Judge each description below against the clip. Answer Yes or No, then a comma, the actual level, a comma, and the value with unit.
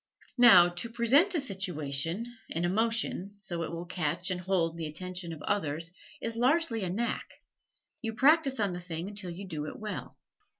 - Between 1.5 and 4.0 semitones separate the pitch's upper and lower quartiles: No, average, 5.2 semitones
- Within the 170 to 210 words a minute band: Yes, average, 175 wpm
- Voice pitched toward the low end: No, medium, 185 Hz